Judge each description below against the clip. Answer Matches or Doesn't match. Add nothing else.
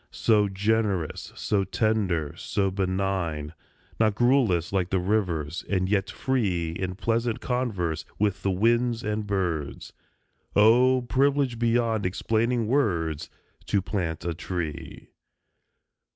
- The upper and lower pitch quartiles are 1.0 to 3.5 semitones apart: Doesn't match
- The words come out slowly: Matches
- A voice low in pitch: Matches